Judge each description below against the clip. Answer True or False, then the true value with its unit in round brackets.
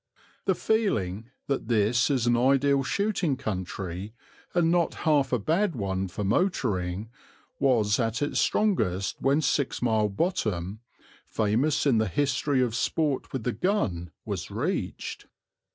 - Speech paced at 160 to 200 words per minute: False (135 wpm)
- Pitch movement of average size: False (6.0 semitones)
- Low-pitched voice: True (125 Hz)